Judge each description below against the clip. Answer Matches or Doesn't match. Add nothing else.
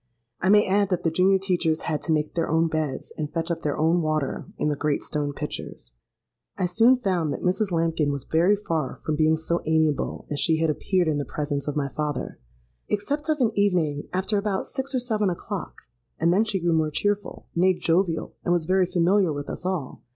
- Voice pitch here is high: Doesn't match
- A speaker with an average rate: Doesn't match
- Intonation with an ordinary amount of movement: Matches